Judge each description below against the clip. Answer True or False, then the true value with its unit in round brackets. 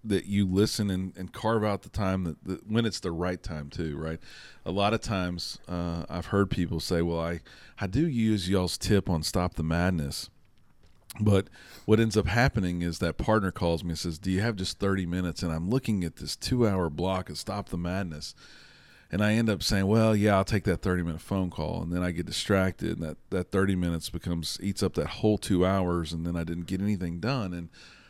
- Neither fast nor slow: False (230 wpm)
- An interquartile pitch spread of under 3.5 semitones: True (2.9 semitones)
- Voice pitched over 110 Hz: False (95 Hz)